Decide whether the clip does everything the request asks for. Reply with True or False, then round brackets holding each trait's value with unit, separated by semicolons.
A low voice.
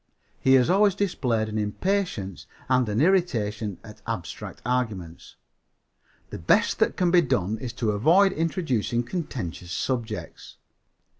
True (120 Hz)